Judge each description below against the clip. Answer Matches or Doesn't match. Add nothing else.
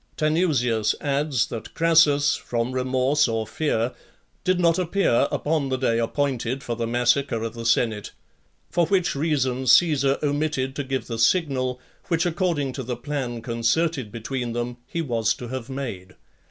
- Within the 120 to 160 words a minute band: Matches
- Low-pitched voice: Matches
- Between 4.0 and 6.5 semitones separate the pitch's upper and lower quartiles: Matches